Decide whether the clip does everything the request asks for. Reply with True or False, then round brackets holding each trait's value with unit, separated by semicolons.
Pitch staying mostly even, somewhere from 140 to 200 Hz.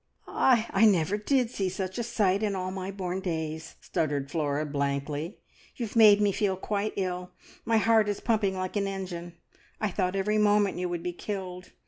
False (3.0 semitones; 190 Hz)